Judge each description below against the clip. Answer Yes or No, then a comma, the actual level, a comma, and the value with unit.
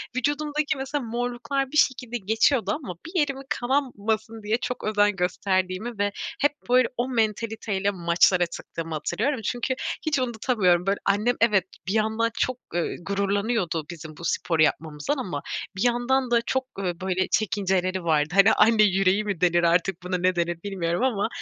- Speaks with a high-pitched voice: Yes, high, 210 Hz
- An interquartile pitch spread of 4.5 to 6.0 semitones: Yes, average, 5.0 semitones